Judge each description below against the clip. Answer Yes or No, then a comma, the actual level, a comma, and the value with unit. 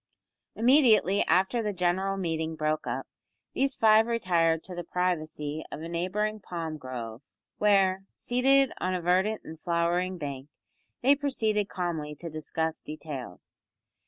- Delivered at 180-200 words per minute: No, slow, 135 wpm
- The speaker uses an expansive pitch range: No, average, 5.0 semitones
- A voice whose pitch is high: No, medium, 180 Hz